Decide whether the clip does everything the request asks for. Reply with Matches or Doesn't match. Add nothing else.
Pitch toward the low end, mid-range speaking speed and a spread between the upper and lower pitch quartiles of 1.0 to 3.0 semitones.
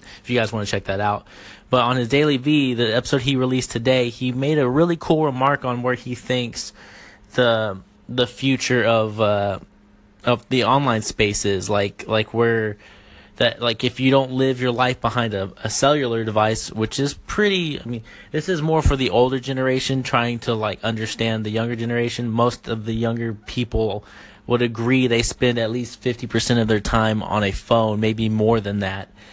Matches